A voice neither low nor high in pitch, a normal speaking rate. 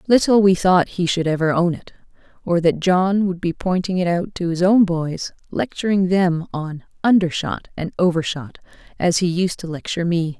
Yes: medium, 175 Hz; average, 185 wpm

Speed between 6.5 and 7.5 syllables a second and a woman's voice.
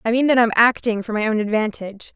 Yes: 6.6 syllables/s; female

